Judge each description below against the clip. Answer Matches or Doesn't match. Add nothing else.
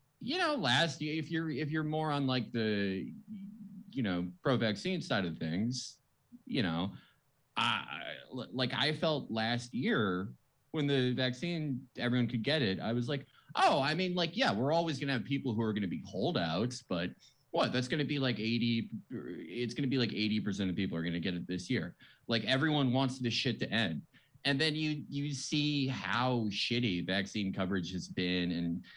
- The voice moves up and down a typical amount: Doesn't match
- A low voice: Matches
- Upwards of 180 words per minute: Matches